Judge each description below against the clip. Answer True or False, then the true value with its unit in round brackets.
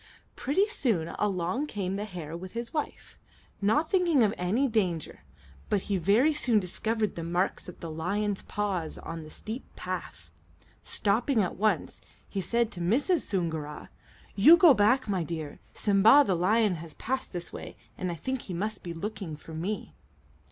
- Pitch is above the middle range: True (200 Hz)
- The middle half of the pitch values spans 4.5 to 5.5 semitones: True (5.1 semitones)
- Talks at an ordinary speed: True (170 wpm)